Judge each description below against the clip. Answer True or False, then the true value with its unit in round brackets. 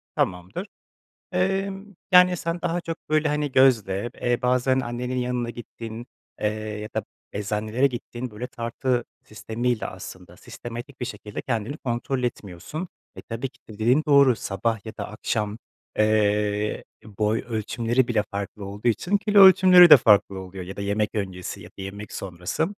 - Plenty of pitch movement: False (4.2 semitones)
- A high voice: False (115 Hz)